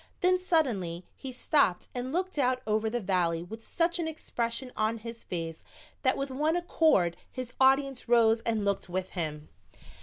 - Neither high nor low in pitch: No, high, 235 Hz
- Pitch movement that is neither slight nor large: No, wide, 6.4 semitones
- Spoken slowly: No, average, 170 wpm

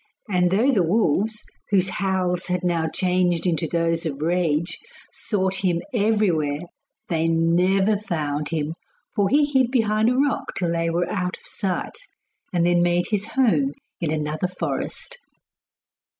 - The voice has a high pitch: No, medium, 180 Hz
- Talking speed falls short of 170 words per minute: Yes, average, 150 wpm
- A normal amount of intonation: Yes, average, 3.8 semitones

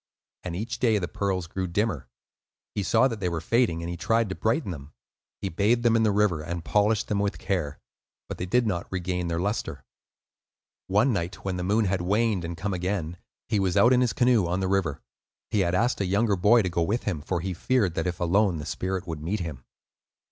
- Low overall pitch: Yes, very low, 95 Hz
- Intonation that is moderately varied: Yes, average, 3.7 semitones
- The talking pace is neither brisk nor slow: No, fast, 225 wpm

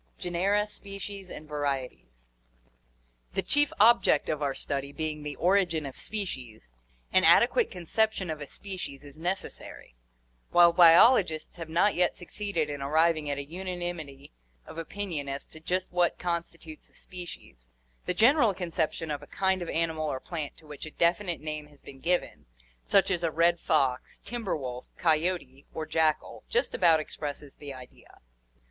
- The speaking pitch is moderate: Yes, medium, 165 Hz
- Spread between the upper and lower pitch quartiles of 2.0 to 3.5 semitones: No, average, 4.0 semitones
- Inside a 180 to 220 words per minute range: No, average, 160 wpm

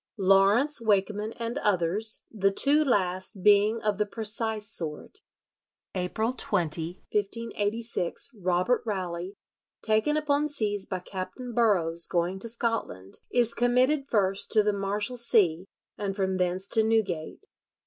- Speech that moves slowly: Yes, slow, 125 wpm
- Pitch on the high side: Yes, high, 205 Hz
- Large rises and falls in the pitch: No, average, 3.7 semitones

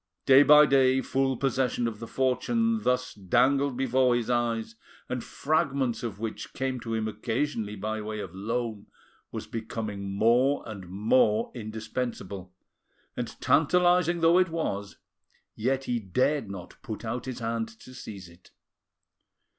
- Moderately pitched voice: No, low, 120 Hz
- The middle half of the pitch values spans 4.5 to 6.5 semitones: No, average, 3.7 semitones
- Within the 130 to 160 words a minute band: Yes, average, 145 wpm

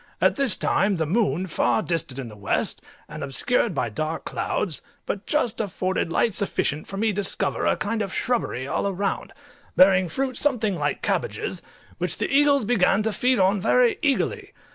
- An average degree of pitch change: No, wide, 6.3 semitones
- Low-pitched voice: No, high, 200 Hz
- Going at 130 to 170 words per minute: No, average, 180 wpm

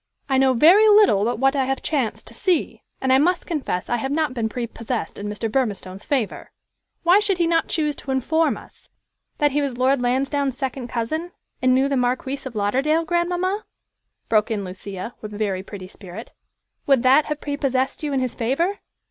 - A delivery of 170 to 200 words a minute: Yes, average, 190 wpm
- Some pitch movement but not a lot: Yes, average, 4.7 semitones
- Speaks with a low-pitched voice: No, very high, 265 Hz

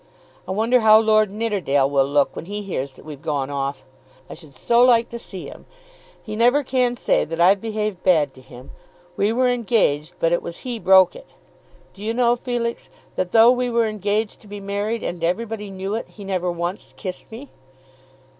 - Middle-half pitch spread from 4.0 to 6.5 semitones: Yes, average, 5.1 semitones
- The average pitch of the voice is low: No, high, 205 Hz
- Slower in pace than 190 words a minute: No, average, 200 wpm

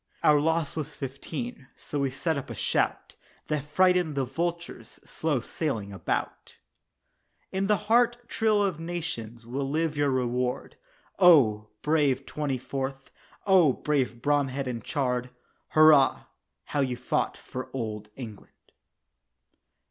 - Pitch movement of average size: Yes, average, 4.4 semitones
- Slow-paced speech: Yes, slow, 130 wpm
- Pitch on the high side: No, medium, 140 Hz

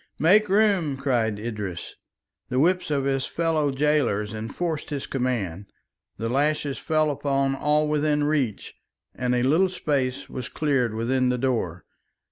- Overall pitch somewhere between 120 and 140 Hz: Yes, low, 135 Hz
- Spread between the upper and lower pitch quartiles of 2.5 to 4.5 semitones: Yes, average, 3.8 semitones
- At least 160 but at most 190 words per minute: No, average, 140 wpm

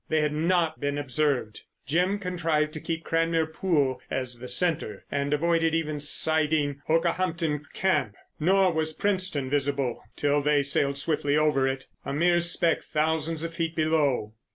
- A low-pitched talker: No, medium, 155 Hz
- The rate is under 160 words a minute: Yes, average, 150 wpm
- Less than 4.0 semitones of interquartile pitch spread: Yes, narrow, 2.6 semitones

